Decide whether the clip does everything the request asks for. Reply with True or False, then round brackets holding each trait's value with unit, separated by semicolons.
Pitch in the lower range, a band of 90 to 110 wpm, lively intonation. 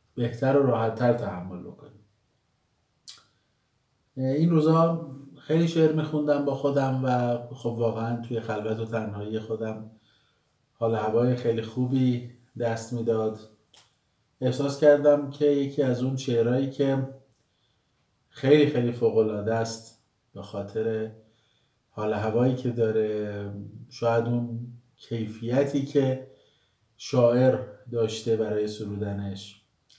False (120 Hz; 105 wpm; 3.2 semitones)